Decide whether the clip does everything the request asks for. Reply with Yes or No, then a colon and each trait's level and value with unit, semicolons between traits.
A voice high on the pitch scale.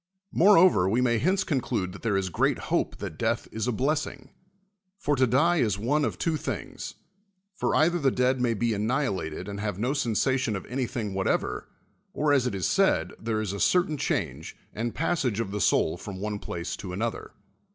No: low, 120 Hz